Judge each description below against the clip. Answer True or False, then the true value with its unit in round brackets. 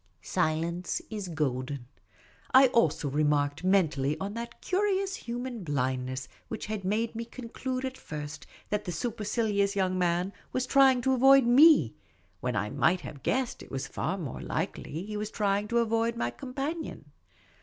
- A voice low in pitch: False (205 Hz)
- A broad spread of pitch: True (7.8 semitones)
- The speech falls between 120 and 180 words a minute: True (160 wpm)